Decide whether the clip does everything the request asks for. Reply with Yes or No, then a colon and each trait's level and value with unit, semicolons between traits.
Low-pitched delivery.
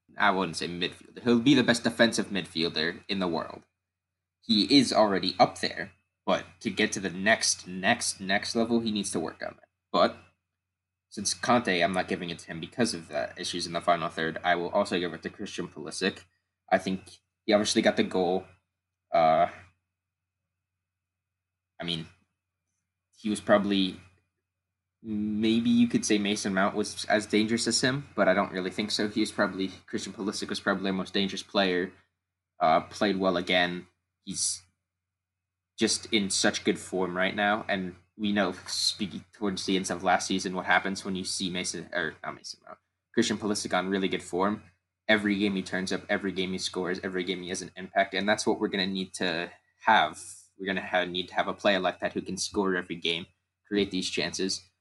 Yes: very low, 95 Hz